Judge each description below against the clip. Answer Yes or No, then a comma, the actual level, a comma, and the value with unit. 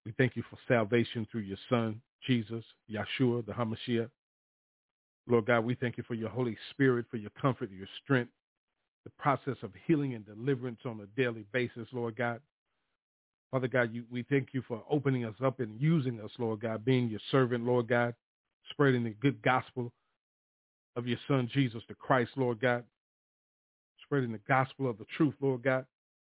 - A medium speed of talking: Yes, average, 175 wpm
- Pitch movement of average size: No, narrow, 2.3 semitones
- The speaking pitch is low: Yes, low, 120 Hz